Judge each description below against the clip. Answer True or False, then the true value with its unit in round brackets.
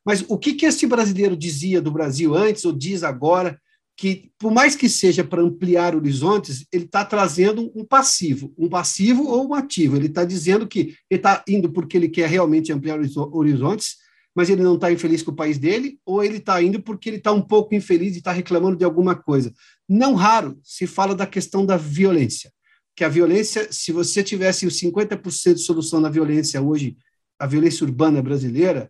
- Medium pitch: True (180 Hz)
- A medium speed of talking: False (190 wpm)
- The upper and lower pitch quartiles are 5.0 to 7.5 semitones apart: False (4.3 semitones)